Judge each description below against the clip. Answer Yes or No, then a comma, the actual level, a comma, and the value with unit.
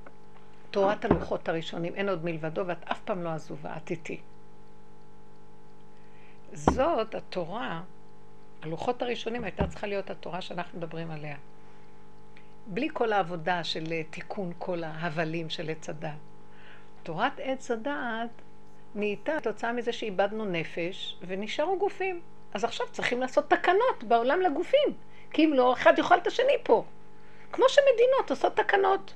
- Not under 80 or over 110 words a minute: No, average, 130 wpm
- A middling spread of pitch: No, wide, 7.5 semitones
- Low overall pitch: No, high, 215 Hz